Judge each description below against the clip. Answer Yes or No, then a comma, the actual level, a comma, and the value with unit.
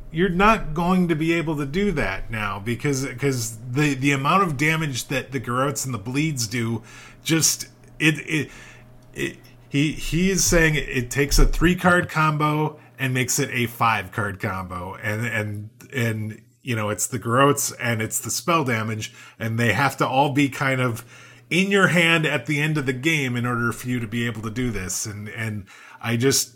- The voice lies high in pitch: No, low, 130 Hz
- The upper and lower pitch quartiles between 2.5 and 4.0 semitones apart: No, average, 4.5 semitones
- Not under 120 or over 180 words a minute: No, average, 200 wpm